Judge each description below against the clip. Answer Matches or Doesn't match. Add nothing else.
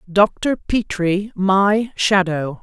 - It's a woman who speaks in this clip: Matches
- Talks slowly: Matches